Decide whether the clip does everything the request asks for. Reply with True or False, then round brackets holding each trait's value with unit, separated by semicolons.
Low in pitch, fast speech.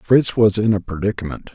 False (105 Hz; 195 wpm)